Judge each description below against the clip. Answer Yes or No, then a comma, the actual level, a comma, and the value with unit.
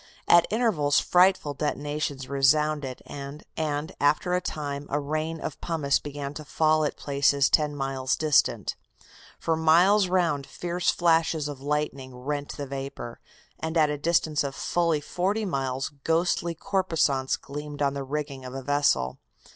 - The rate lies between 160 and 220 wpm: No, average, 145 wpm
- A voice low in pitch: No, medium, 150 Hz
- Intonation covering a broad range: No, average, 2.7 semitones